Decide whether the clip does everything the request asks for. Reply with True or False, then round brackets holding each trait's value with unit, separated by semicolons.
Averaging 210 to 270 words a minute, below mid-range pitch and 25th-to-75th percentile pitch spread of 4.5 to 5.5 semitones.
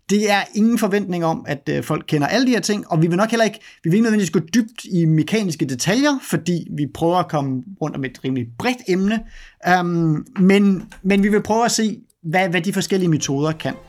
False (220 wpm; 185 Hz; 4.9 semitones)